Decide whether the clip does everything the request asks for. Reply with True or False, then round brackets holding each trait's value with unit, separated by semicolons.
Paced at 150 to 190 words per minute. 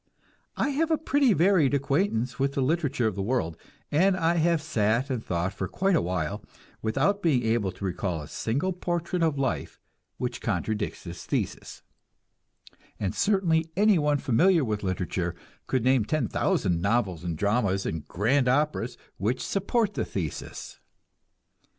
True (155 wpm)